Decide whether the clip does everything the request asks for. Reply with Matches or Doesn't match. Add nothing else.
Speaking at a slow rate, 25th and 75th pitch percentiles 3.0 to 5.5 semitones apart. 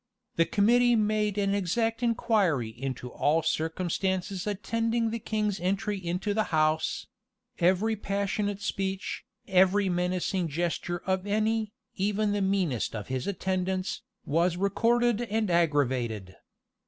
Matches